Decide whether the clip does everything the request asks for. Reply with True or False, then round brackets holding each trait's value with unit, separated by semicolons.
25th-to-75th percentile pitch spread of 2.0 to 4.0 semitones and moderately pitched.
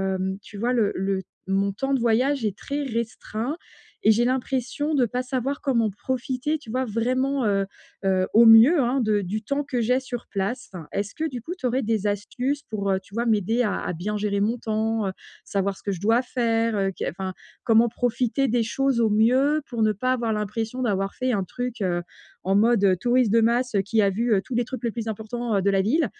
False (3.7 semitones; 230 Hz)